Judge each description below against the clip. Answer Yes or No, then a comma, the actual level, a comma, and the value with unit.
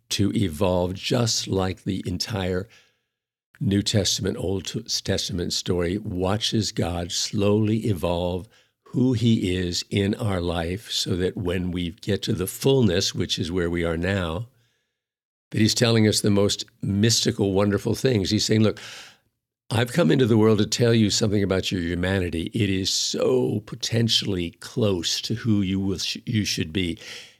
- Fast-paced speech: No, average, 155 wpm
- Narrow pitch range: No, average, 3.3 semitones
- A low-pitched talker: Yes, low, 100 Hz